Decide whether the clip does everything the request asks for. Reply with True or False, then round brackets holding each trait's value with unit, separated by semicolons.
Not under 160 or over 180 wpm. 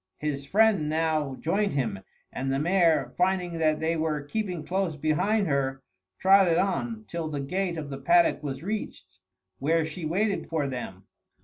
True (165 wpm)